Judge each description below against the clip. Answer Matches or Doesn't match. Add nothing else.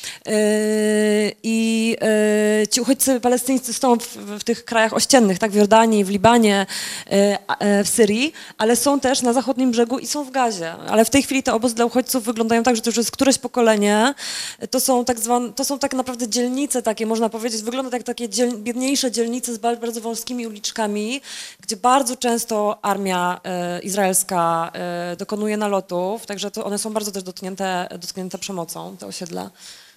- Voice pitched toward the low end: Doesn't match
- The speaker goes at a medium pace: Doesn't match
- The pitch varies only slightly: Doesn't match